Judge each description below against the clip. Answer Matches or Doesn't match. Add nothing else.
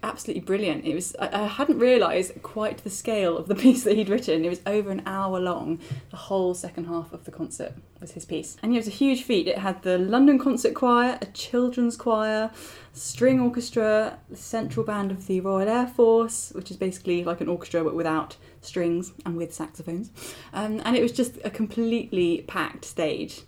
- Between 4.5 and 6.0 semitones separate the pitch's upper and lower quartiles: Matches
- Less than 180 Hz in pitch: Doesn't match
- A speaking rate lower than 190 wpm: Doesn't match